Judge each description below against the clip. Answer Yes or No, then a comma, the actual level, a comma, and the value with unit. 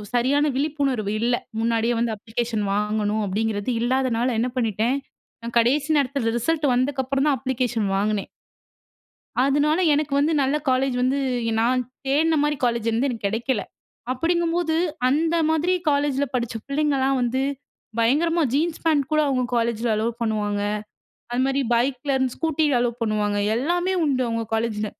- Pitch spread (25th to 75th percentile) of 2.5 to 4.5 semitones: Yes, average, 3.9 semitones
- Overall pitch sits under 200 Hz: No, very high, 255 Hz